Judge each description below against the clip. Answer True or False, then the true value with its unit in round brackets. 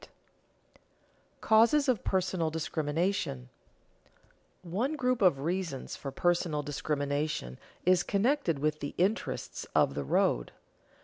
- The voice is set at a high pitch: False (170 Hz)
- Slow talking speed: True (110 wpm)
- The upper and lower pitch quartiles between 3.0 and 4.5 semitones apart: False (5.3 semitones)